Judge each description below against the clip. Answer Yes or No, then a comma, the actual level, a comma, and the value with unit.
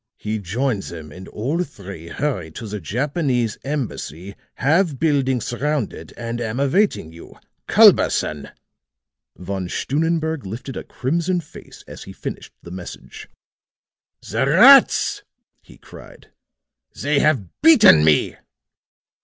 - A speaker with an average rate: No, slow, 120 wpm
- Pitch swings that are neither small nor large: No, wide, 7.9 semitones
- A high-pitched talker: No, low, 120 Hz